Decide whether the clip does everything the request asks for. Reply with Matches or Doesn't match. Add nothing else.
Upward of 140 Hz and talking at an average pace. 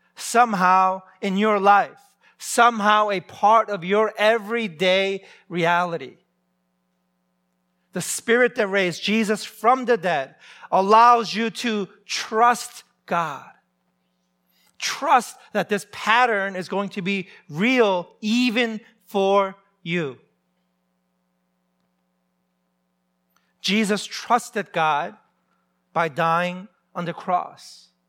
Doesn't match